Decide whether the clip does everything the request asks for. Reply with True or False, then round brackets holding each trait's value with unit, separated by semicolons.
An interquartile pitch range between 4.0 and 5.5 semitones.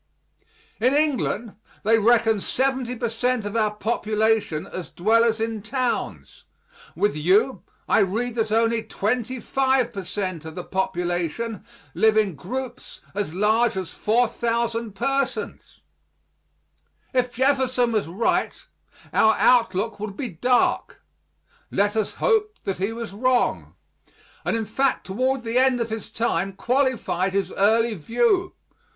False (3.6 semitones)